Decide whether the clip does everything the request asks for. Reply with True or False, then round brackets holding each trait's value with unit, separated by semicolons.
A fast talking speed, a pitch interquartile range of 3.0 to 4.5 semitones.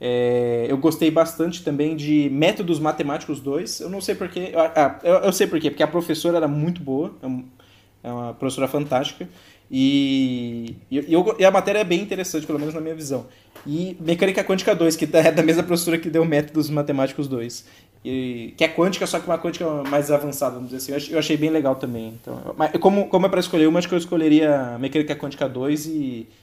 True (205 wpm; 4.0 semitones)